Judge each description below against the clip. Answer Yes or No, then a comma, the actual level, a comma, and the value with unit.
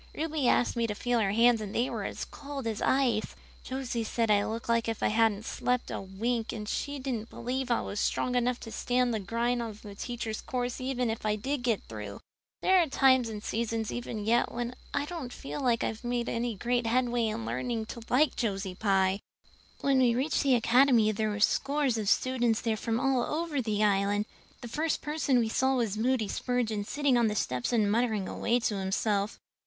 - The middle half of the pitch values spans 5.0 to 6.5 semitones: No, average, 2.8 semitones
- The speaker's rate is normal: No, fast, 210 wpm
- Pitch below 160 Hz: No, high, 235 Hz